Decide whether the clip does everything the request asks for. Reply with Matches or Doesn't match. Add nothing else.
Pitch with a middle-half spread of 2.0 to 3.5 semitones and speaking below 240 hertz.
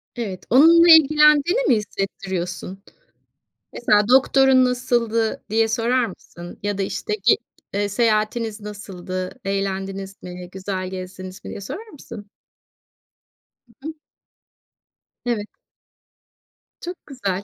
Doesn't match